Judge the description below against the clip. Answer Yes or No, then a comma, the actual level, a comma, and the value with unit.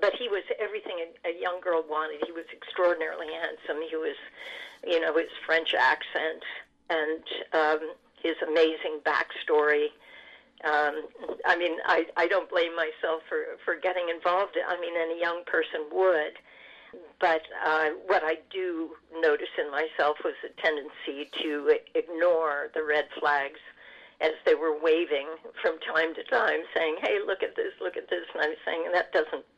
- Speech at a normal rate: Yes, average, 160 wpm